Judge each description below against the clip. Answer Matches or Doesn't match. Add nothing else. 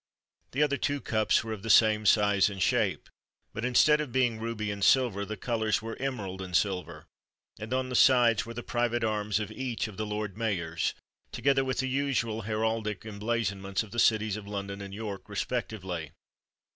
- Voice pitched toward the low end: Matches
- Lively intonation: Doesn't match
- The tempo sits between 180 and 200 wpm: Matches